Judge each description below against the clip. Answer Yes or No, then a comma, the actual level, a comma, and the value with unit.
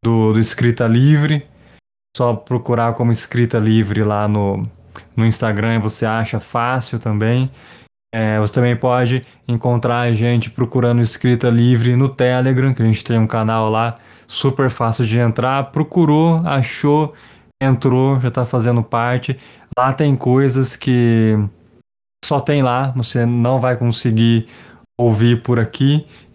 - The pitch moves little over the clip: Yes, narrow, 2.3 semitones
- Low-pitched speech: Yes, low, 120 Hz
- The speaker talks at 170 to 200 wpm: No, average, 140 wpm